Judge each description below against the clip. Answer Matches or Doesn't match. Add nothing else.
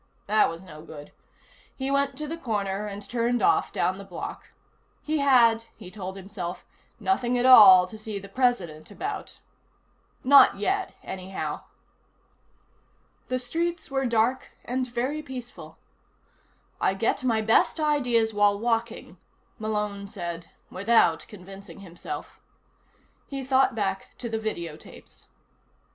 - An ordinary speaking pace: Doesn't match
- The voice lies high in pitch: Matches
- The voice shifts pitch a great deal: Doesn't match